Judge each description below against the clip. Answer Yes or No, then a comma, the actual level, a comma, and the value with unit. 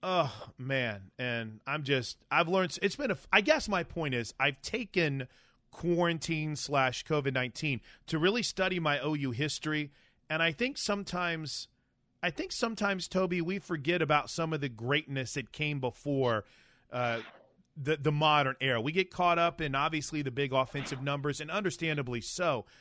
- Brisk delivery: No, average, 165 wpm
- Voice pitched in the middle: Yes, medium, 150 Hz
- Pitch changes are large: No, average, 4.6 semitones